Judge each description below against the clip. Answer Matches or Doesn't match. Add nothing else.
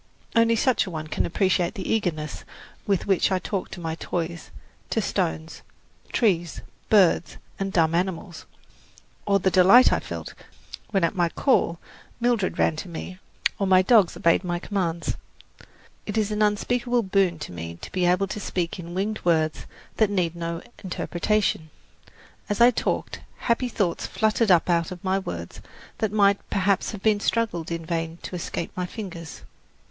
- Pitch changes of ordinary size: Matches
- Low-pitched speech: Doesn't match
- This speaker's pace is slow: Doesn't match